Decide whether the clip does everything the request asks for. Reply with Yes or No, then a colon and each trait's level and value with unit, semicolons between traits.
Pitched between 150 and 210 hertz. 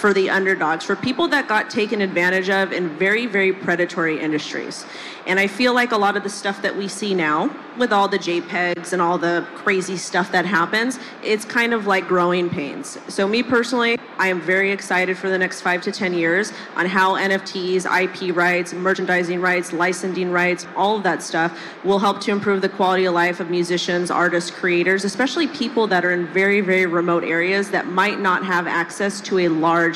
Yes: medium, 185 Hz